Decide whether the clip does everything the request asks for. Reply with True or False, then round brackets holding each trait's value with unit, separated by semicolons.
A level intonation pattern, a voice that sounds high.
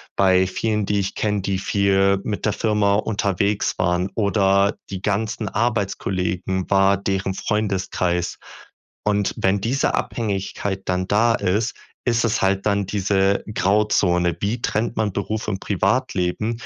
False (1.8 semitones; 100 Hz)